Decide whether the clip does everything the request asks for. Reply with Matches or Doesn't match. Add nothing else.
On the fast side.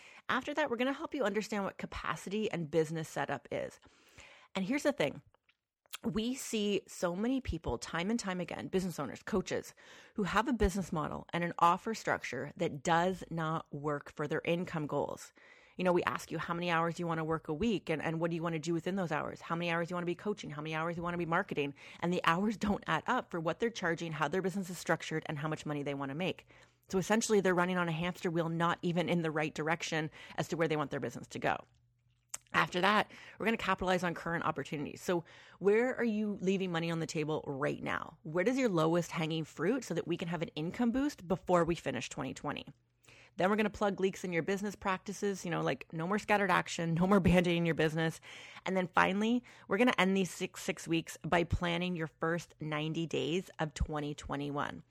Matches